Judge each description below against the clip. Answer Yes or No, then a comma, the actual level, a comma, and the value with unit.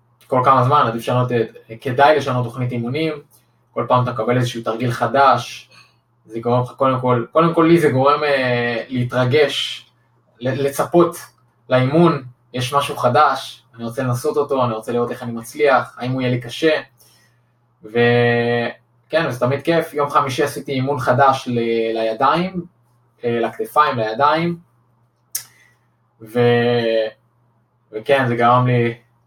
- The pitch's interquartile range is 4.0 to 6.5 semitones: No, average, 2.9 semitones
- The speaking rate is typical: Yes, average, 135 wpm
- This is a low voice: Yes, low, 125 Hz